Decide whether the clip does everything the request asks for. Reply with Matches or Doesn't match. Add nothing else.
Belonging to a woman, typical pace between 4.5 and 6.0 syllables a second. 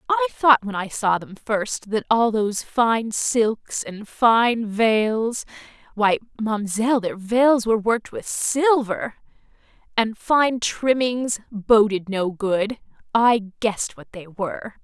Doesn't match